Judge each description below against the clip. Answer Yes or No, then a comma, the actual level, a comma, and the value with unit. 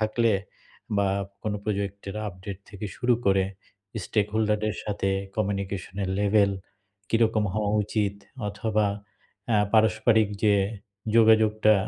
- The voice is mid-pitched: No, low, 105 Hz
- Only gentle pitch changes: Yes, narrow, 1.5 semitones